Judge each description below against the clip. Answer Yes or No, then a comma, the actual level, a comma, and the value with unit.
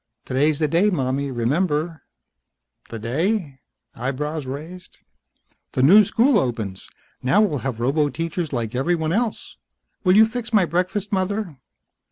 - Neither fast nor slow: No, slow, 130 wpm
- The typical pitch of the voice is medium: Yes, medium, 155 Hz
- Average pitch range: No, wide, 6.1 semitones